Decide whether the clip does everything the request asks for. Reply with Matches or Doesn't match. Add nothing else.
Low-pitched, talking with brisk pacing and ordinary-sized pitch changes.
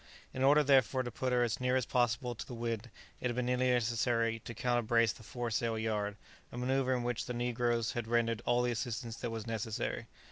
Doesn't match